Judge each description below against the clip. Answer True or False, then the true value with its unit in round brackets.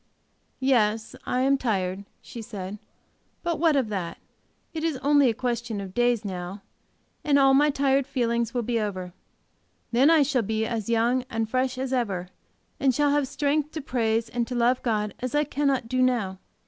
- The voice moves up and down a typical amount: True (3.9 semitones)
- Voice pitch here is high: True (245 Hz)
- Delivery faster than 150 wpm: True (185 wpm)